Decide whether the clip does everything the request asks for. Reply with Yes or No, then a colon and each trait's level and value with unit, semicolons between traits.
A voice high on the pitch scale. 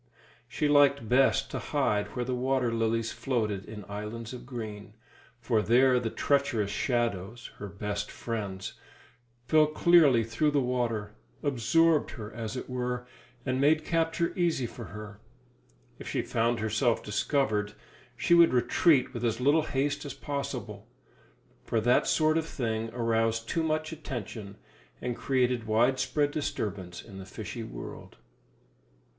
No: low, 120 Hz